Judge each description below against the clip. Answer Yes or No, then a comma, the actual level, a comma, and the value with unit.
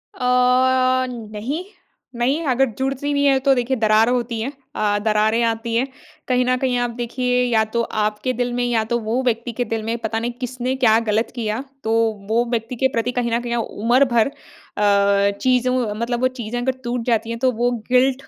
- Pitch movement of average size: No, narrow, 2.0 semitones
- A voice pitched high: Yes, high, 240 Hz